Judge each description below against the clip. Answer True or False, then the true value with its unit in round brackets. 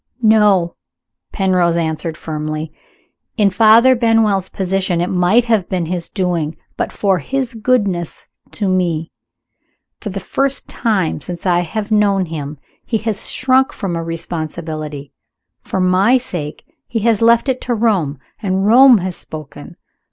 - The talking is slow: False (145 wpm)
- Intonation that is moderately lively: True (4.7 semitones)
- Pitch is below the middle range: False (190 Hz)